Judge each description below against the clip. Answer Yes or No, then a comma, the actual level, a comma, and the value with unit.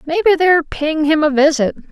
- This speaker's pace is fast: Yes, fast, 220 wpm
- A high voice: Yes, very high, 310 Hz